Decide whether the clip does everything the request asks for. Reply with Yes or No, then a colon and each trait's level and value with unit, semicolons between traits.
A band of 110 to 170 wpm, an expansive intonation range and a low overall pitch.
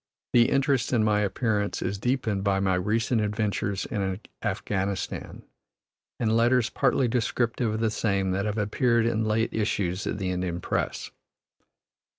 No: average, 150 wpm; average, 2.8 semitones; low, 105 Hz